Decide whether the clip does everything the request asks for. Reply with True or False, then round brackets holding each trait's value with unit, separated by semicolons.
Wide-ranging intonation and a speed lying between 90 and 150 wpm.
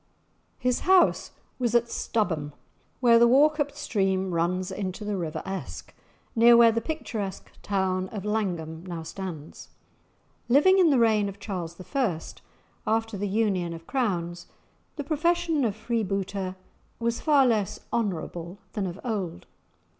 False (4.5 semitones; 140 wpm)